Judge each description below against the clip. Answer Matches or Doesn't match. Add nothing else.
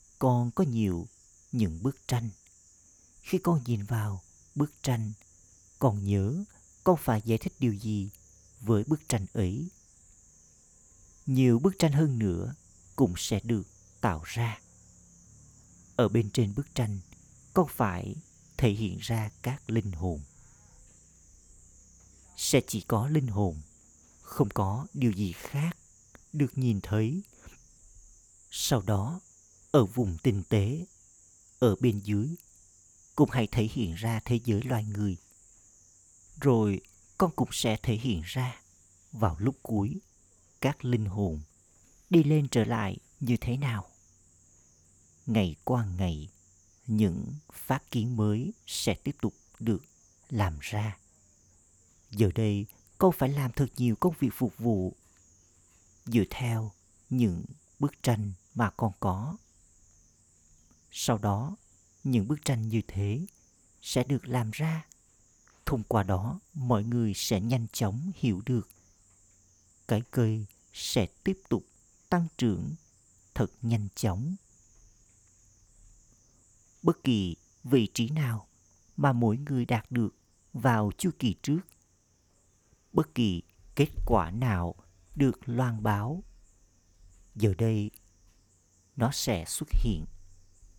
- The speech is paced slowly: Matches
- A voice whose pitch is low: Matches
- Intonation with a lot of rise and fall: Doesn't match